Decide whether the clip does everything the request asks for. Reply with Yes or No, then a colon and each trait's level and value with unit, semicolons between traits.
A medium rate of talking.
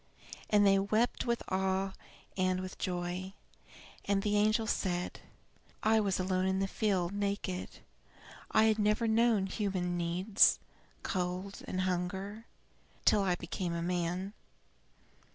No: slow, 130 wpm